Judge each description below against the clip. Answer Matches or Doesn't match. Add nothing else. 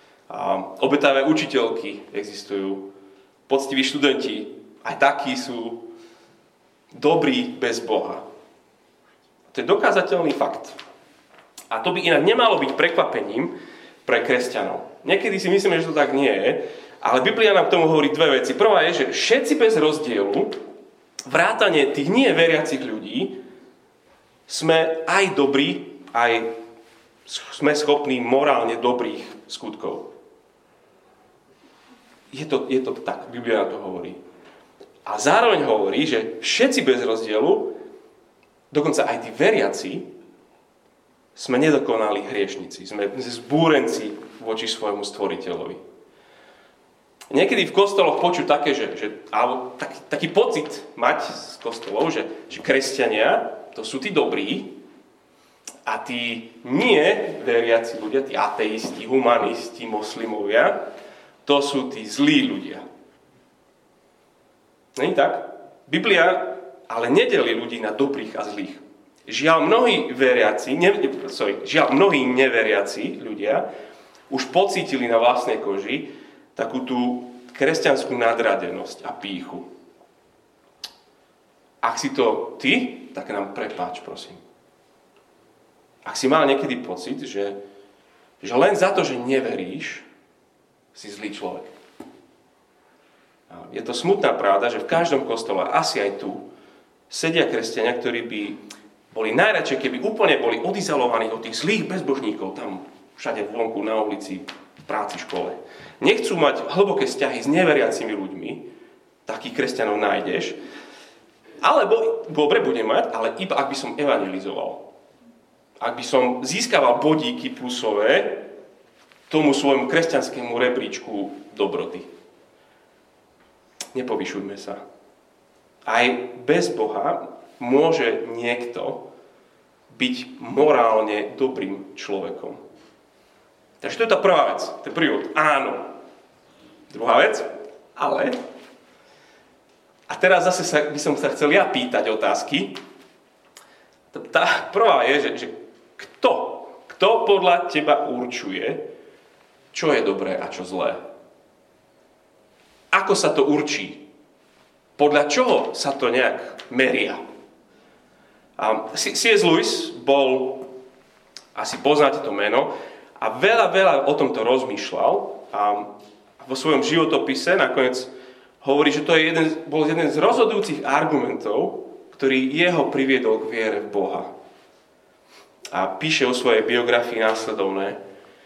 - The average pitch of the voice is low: Doesn't match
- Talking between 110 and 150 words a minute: Matches